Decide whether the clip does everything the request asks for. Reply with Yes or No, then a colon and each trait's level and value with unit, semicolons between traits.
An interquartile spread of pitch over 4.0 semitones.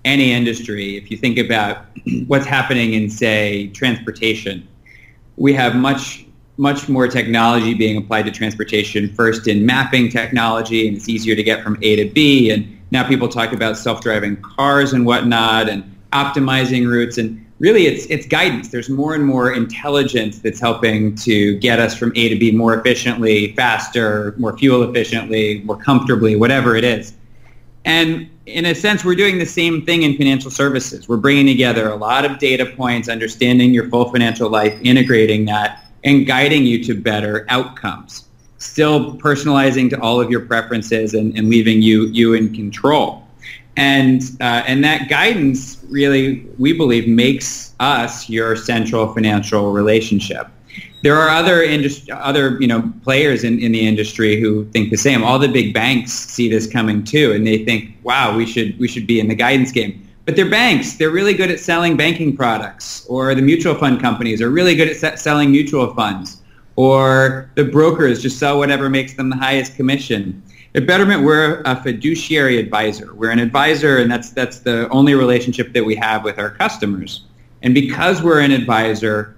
No: average, 3.6 semitones